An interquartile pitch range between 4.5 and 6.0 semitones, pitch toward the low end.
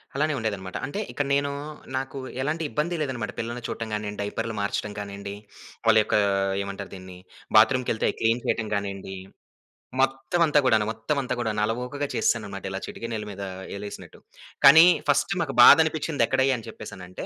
Yes: average, 5.1 semitones; low, 115 Hz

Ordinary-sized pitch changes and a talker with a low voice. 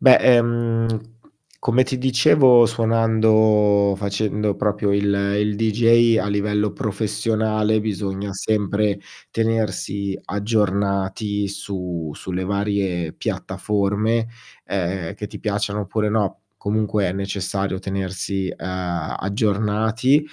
No: narrow, 2.0 semitones; low, 105 Hz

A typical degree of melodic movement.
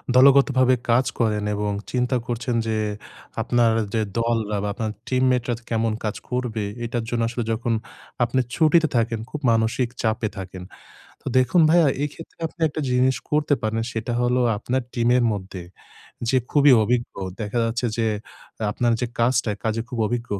No: narrow, 2.3 semitones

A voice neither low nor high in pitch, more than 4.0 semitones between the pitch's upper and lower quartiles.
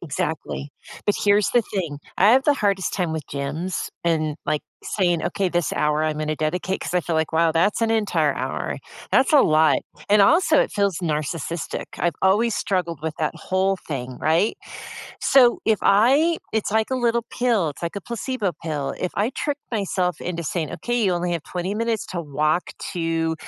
Yes: medium, 180 Hz; average, 5.1 semitones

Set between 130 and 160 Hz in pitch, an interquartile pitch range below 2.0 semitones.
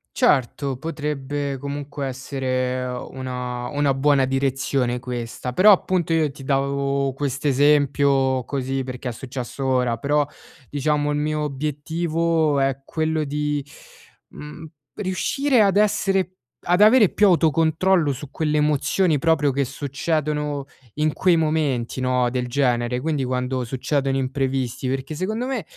No: medium, 140 Hz; average, 2.8 semitones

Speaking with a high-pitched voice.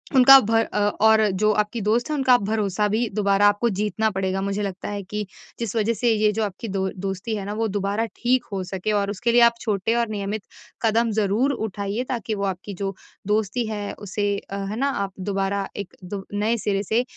Yes: high, 210 Hz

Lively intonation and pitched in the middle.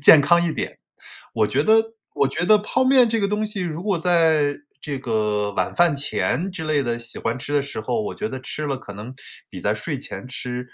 Yes: wide, 7.0 semitones; medium, 145 Hz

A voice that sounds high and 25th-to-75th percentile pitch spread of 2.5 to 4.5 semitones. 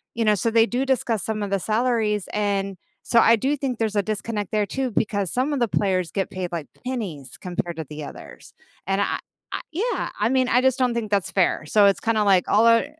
Yes: high, 215 Hz; average, 3.4 semitones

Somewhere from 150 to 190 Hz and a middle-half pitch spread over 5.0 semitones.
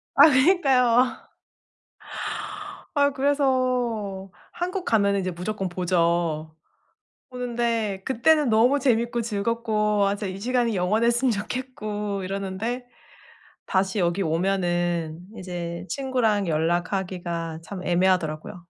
No: high, 205 Hz; wide, 5.4 semitones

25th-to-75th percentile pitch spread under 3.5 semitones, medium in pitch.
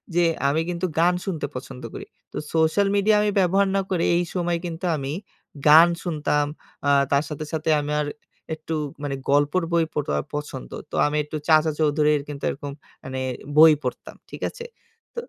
Yes: average, 2.9 semitones; medium, 155 Hz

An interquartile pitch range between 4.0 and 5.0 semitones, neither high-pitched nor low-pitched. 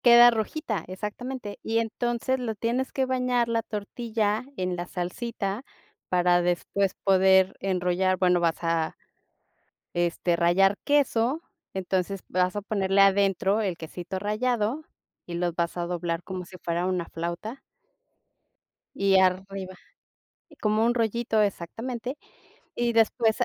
No: average, 4.3 semitones; high, 195 Hz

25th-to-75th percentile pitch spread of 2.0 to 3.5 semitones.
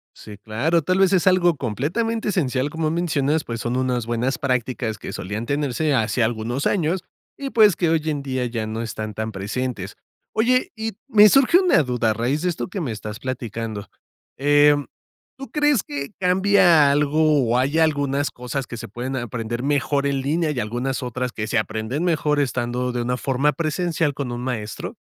No: average, 5.2 semitones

